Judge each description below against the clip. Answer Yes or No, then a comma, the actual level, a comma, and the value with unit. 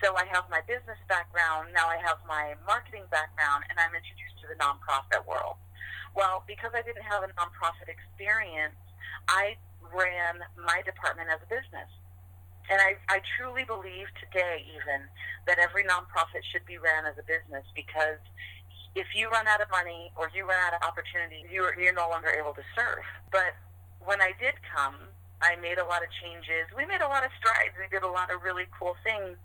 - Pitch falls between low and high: Yes, medium, 165 Hz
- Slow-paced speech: No, average, 195 wpm